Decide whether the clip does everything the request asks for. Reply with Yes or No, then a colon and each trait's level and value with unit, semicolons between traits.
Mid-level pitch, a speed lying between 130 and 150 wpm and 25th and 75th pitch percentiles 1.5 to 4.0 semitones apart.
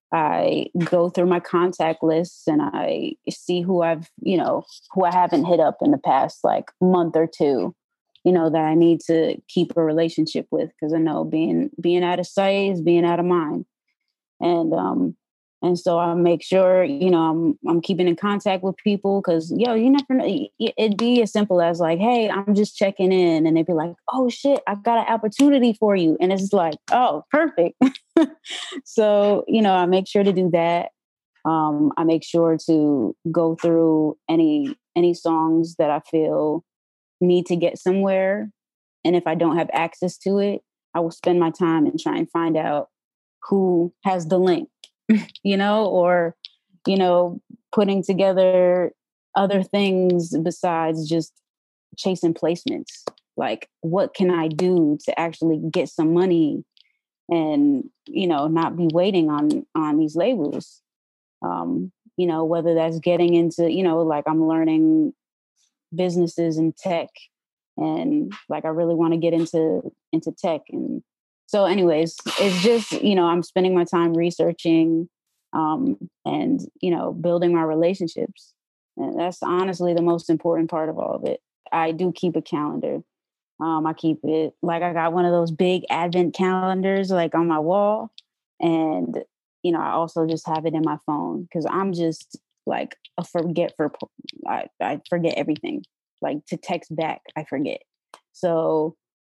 No: medium, 175 Hz; average, 170 wpm; average, 3.2 semitones